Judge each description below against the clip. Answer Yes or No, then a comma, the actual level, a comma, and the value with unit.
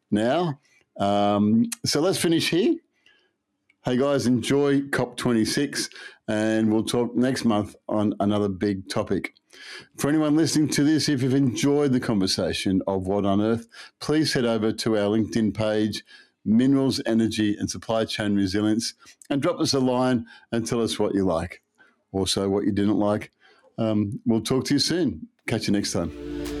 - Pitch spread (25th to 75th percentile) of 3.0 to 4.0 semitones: No, average, 5.0 semitones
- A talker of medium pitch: No, low, 115 Hz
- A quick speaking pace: No, average, 160 wpm